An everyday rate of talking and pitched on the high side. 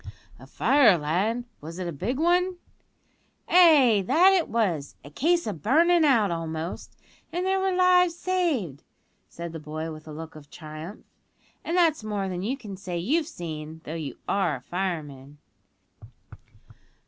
Yes: average, 160 wpm; high, 195 Hz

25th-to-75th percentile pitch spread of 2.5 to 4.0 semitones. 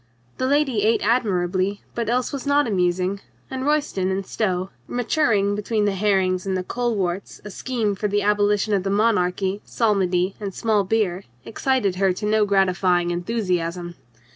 Yes: average, 3.4 semitones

